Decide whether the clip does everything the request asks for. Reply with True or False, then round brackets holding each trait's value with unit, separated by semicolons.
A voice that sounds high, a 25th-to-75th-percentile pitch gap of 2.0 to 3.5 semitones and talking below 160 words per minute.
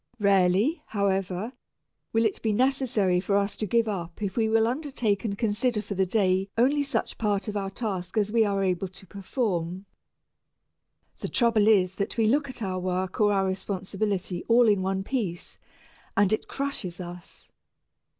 False (200 Hz; 3.2 semitones; 170 wpm)